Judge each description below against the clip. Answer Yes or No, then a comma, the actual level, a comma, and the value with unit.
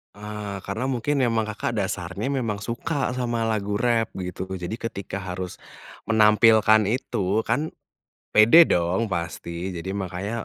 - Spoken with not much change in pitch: No, average, 3.6 semitones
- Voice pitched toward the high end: No, low, 105 Hz